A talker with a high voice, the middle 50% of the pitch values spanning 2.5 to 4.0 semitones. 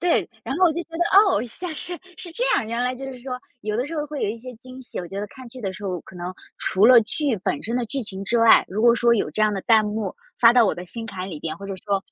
No: high, 230 Hz; average, 4.4 semitones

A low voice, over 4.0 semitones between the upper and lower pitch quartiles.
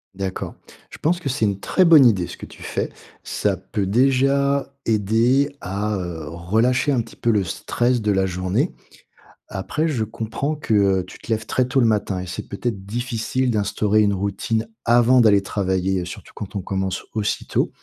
Yes: low, 110 Hz; average, 4.5 semitones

